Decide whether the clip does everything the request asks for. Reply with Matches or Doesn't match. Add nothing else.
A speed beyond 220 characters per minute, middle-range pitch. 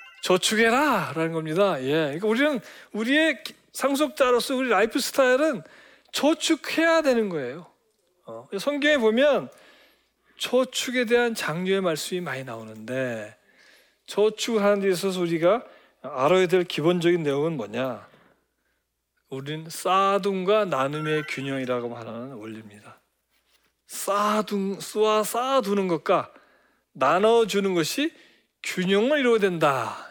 Doesn't match